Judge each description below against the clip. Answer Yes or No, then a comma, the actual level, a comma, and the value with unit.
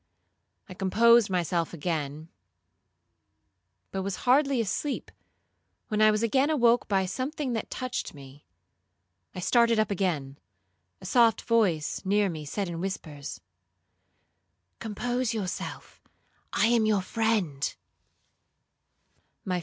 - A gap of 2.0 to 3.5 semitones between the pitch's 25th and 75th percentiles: No, average, 5.1 semitones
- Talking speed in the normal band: No, slow, 110 wpm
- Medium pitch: No, high, 205 Hz